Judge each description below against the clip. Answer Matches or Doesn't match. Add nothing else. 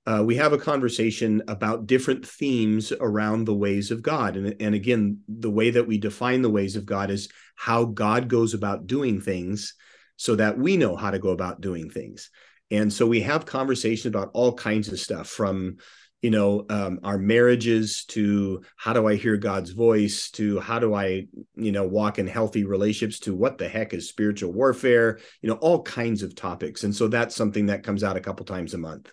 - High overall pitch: Doesn't match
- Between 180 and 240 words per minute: Matches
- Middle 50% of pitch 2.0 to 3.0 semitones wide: Matches